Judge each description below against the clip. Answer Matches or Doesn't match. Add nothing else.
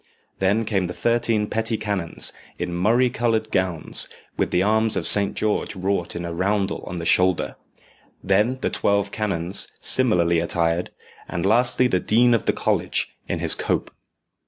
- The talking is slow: Doesn't match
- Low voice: Matches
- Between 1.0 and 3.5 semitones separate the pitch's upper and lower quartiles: Doesn't match